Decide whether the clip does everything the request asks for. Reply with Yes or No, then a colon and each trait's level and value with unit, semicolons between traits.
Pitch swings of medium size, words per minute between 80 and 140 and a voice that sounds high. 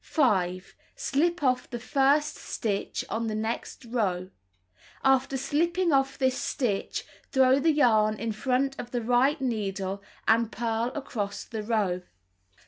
Yes: average, 4.1 semitones; slow, 135 wpm; high, 245 Hz